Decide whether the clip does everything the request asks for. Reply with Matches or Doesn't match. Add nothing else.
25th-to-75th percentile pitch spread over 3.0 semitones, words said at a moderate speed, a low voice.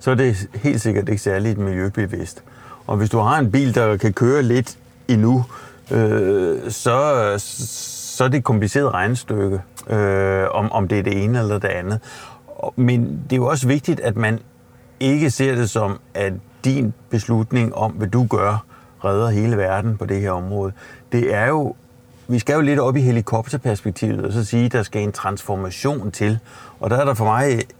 Matches